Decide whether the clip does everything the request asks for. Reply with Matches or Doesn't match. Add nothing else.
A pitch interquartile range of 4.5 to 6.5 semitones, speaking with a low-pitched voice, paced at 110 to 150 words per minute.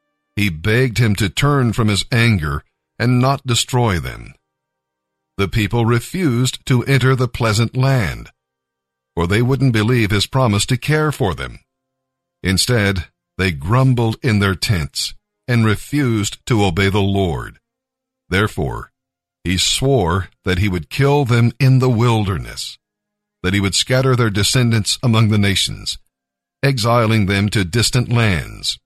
Matches